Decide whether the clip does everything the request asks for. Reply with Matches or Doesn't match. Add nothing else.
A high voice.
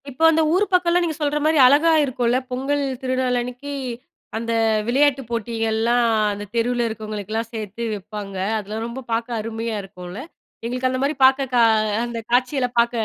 Matches